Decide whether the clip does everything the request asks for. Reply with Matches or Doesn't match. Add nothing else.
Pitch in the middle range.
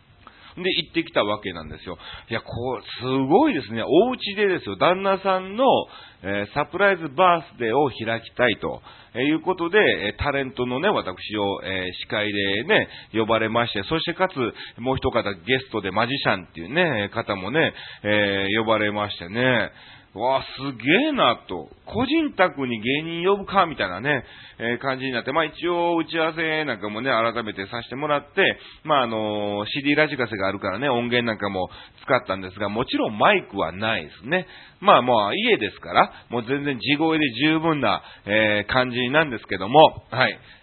Doesn't match